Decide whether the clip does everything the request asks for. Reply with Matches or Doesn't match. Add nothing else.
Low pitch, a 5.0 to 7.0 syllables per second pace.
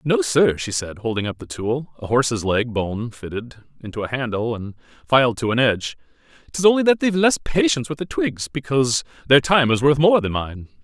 Matches